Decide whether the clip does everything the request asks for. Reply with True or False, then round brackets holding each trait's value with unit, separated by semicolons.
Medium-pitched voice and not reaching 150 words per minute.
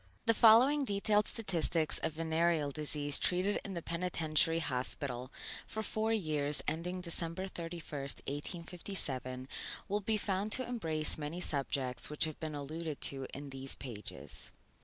True (165 Hz; 140 wpm)